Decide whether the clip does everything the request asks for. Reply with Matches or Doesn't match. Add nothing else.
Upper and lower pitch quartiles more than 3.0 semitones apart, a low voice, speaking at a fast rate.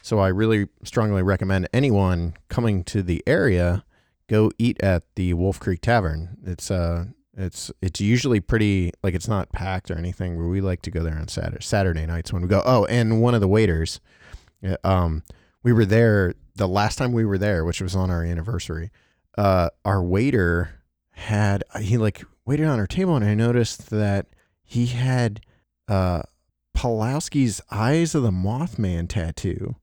Doesn't match